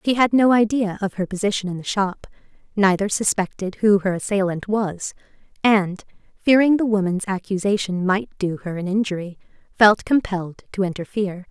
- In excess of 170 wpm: No, average, 155 wpm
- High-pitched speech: Yes, high, 200 Hz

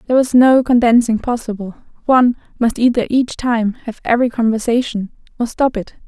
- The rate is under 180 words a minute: Yes, average, 160 wpm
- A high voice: Yes, high, 235 Hz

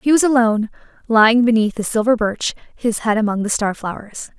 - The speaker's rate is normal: Yes, average, 190 wpm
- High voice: Yes, high, 225 Hz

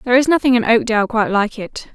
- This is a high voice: Yes, high, 235 Hz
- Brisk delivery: Yes, fast, 245 wpm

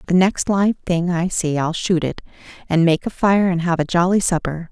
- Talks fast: Yes, fast, 230 wpm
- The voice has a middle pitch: Yes, medium, 175 Hz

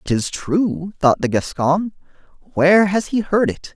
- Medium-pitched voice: Yes, medium, 170 Hz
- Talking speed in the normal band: Yes, average, 160 wpm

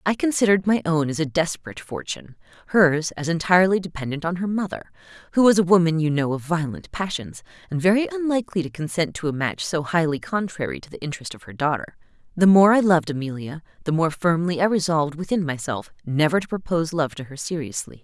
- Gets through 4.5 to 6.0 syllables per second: No, 6.3 syllables/s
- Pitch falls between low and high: Yes, medium, 165 Hz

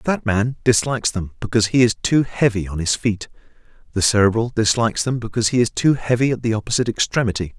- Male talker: Yes, male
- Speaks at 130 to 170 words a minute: No, fast, 205 wpm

